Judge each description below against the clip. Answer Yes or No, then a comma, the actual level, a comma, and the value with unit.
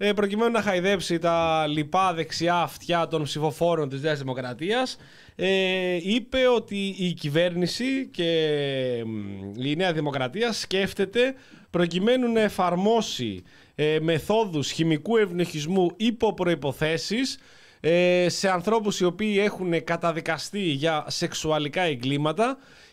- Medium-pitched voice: Yes, medium, 175 Hz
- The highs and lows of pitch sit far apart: No, average, 4.8 semitones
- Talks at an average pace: No, slow, 100 wpm